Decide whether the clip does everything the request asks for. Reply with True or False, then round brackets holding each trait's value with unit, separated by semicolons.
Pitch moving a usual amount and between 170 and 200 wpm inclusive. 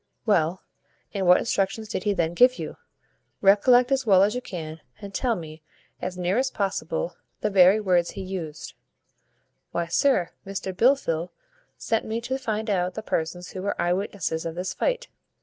True (4.0 semitones; 175 wpm)